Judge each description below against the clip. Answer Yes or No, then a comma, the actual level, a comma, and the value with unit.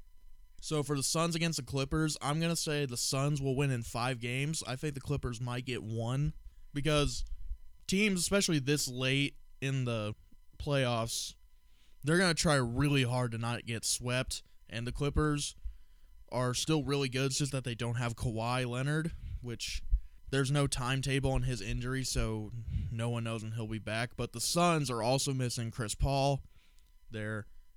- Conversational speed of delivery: Yes, average, 175 wpm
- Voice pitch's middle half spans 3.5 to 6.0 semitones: Yes, average, 4.0 semitones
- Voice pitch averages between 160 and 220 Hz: No, low, 125 Hz